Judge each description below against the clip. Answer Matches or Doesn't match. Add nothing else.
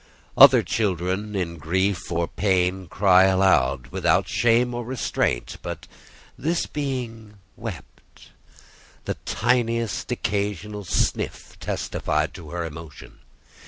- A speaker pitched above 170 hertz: Doesn't match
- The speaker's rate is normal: Doesn't match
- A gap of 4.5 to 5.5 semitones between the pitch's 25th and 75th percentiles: Matches